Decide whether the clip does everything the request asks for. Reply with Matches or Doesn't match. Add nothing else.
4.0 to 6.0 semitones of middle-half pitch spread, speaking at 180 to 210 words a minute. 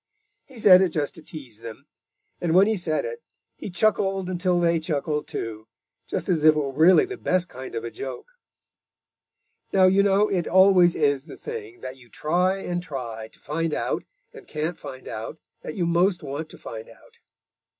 Matches